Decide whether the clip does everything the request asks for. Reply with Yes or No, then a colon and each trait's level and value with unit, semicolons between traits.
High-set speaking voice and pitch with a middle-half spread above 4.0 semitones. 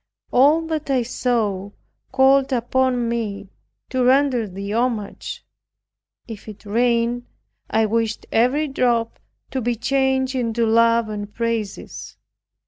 No: high, 235 Hz; average, 2.8 semitones